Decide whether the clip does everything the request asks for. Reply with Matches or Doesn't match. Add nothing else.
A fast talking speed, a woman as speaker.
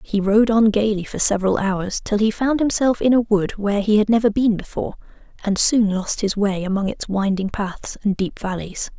Matches